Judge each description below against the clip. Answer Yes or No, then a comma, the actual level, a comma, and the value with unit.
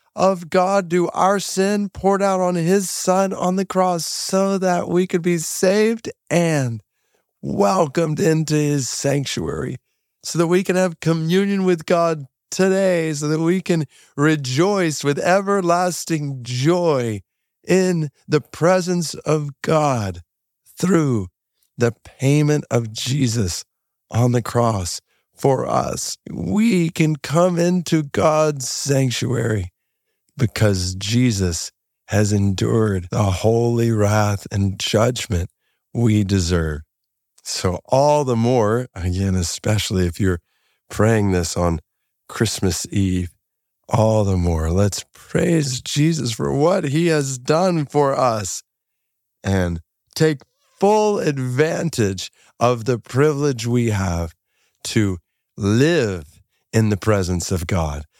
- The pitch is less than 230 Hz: Yes, low, 135 Hz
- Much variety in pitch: Yes, wide, 8.5 semitones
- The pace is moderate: No, slow, 120 wpm